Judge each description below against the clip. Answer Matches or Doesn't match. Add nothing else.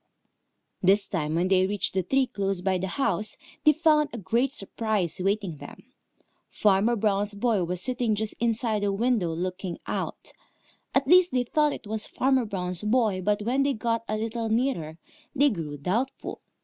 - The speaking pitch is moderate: Doesn't match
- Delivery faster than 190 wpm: Doesn't match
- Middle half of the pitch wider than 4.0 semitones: Matches